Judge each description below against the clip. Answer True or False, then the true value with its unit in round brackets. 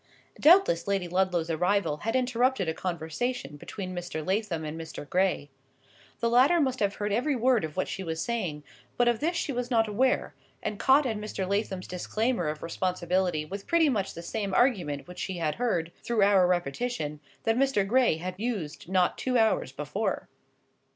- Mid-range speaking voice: False (195 Hz)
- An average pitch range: False (6.0 semitones)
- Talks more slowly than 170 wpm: False (180 wpm)